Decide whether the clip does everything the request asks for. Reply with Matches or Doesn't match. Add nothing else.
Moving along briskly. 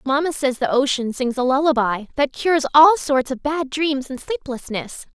Doesn't match